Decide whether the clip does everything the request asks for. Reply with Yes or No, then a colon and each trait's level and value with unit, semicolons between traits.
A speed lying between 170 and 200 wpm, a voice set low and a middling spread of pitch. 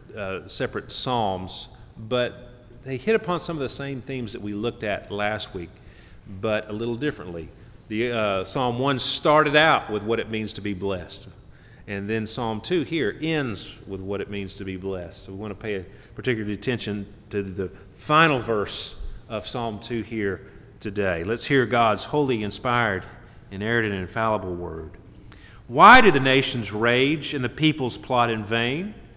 Yes: average, 175 wpm; low, 110 Hz; average, 3.7 semitones